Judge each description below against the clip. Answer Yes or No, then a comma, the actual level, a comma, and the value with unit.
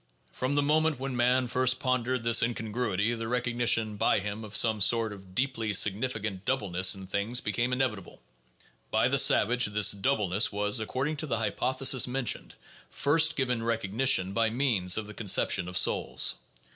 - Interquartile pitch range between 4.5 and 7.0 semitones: No, average, 3.7 semitones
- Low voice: Yes, low, 115 Hz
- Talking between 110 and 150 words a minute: No, average, 165 wpm